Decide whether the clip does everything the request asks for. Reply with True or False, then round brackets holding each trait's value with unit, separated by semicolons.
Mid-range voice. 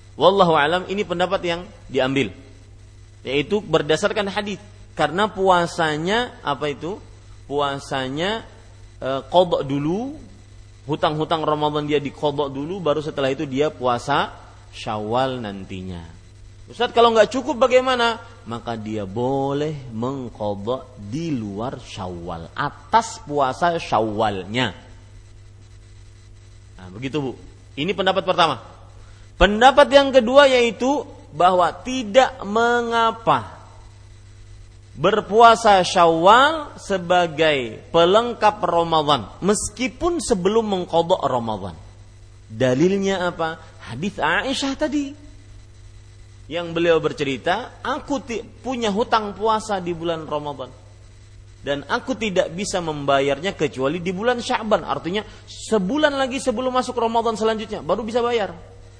True (150 Hz)